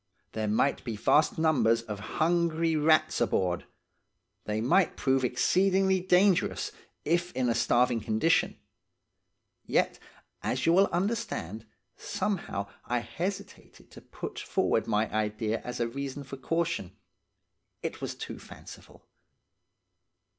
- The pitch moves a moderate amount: No, wide, 7.5 semitones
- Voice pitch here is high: No, low, 135 Hz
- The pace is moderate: No, slow, 120 wpm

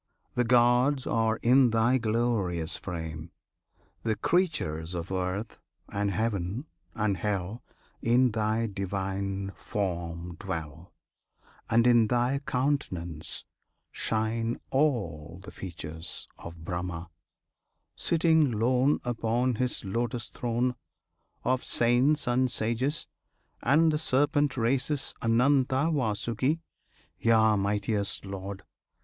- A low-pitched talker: Yes, low, 115 Hz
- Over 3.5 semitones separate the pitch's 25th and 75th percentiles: Yes, average, 4.7 semitones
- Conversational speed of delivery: No, slow, 100 wpm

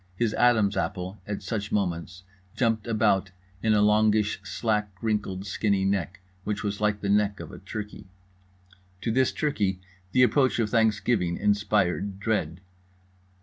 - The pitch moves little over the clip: Yes, narrow, 2.0 semitones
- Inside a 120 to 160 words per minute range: Yes, average, 145 wpm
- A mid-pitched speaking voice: No, low, 105 Hz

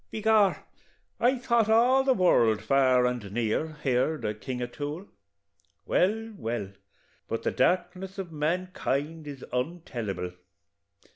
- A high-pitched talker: No, medium, 155 Hz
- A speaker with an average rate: No, slow, 125 wpm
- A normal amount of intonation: No, wide, 7.8 semitones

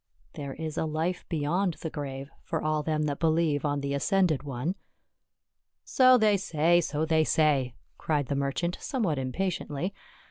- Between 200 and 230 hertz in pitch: No, medium, 155 Hz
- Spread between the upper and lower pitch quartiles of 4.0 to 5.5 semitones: No, average, 3.3 semitones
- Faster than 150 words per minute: Yes, average, 165 wpm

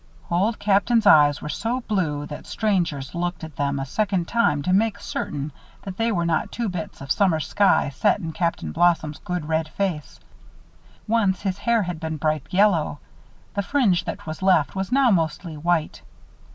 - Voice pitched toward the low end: No, medium, 175 Hz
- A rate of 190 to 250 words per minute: No, average, 180 wpm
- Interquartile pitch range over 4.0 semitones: Yes, average, 4.7 semitones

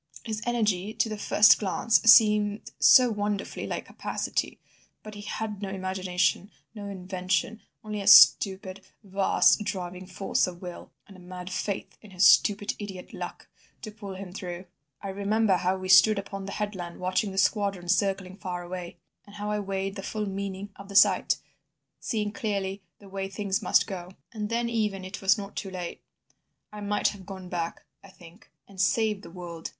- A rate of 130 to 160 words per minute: No, average, 180 wpm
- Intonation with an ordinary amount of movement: No, narrow, 2.0 semitones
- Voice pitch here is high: Yes, high, 195 Hz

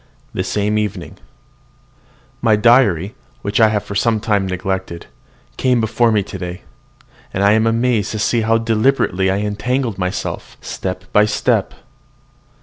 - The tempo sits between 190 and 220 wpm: No, average, 145 wpm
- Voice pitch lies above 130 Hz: No, low, 105 Hz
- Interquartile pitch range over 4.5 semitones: No, average, 2.9 semitones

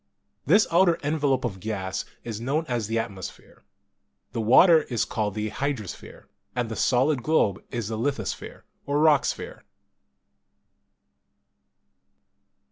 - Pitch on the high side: No, low, 120 Hz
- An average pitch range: Yes, average, 5.0 semitones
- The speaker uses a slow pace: Yes, slow, 125 wpm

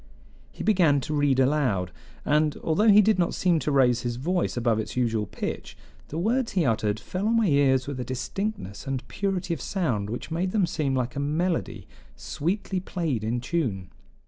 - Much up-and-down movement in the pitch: Yes, wide, 6.7 semitones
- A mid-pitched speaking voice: Yes, medium, 145 Hz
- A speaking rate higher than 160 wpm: Yes, average, 190 wpm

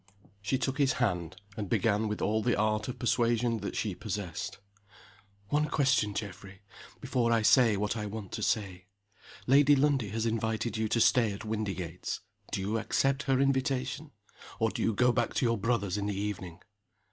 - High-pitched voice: No, low, 110 Hz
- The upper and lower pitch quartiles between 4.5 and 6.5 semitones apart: No, average, 3.4 semitones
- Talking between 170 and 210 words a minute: Yes, average, 180 wpm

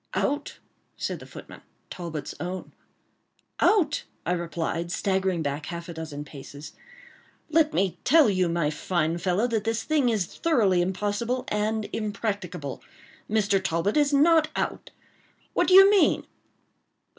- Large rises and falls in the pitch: Yes, wide, 6.5 semitones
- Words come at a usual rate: No, slow, 130 wpm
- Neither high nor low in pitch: No, high, 195 Hz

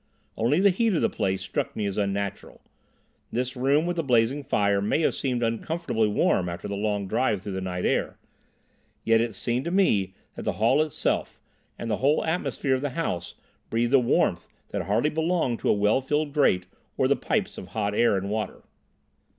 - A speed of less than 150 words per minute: No, average, 195 wpm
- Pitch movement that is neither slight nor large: No, wide, 6.2 semitones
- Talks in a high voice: No, low, 115 Hz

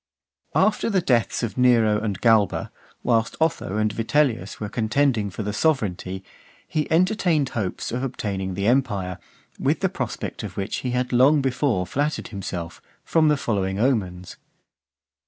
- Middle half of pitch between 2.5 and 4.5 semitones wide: No, wide, 5.5 semitones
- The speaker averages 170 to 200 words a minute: No, average, 155 wpm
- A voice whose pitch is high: No, low, 115 Hz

